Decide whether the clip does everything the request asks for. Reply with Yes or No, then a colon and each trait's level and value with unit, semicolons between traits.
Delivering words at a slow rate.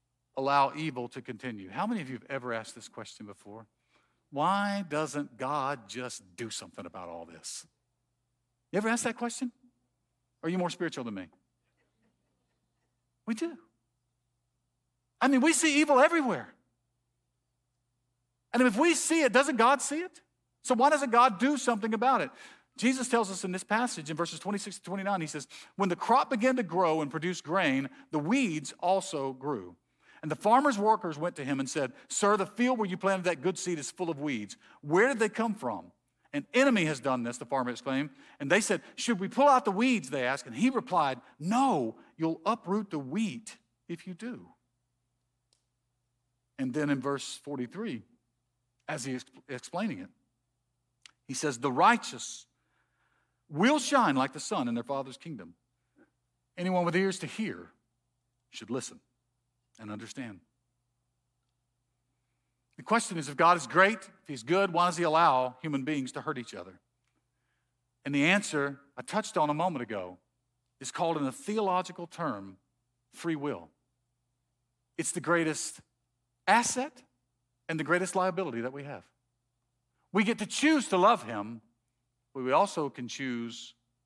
No: average, 165 wpm